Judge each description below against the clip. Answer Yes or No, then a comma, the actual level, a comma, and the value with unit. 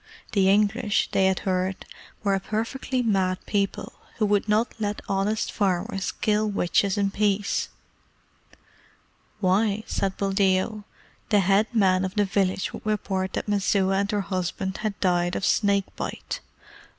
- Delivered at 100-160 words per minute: Yes, average, 145 wpm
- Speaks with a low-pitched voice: No, high, 200 Hz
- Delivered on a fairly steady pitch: Yes, narrow, 1.8 semitones